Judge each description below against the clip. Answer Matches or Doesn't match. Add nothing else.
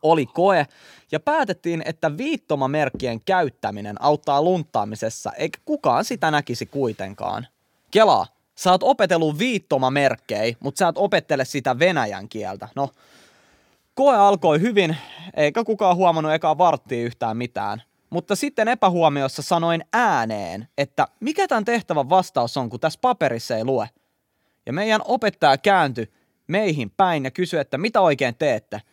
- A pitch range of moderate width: Doesn't match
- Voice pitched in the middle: Matches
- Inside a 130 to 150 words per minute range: Matches